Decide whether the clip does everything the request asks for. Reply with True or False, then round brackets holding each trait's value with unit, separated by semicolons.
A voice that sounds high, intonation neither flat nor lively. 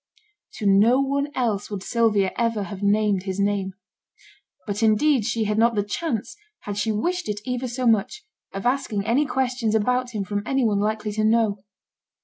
True (220 Hz; 3.4 semitones)